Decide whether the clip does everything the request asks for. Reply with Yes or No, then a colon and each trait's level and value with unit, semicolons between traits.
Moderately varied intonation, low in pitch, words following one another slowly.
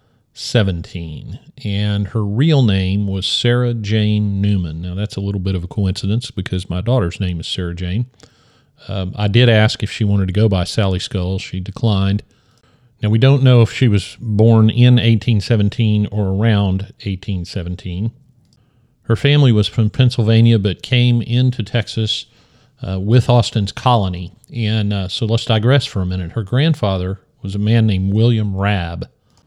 No: average, 3.6 semitones; low, 110 Hz; average, 165 wpm